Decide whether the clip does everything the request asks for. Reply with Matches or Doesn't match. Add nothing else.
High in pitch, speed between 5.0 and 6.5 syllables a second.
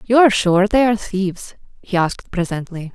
Matches